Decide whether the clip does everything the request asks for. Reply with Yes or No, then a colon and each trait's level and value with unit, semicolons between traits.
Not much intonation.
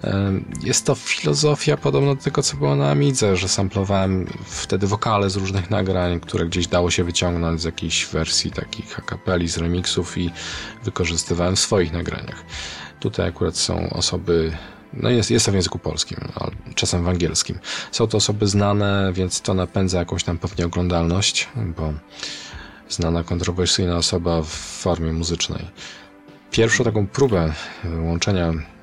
No: average, 3.0 semitones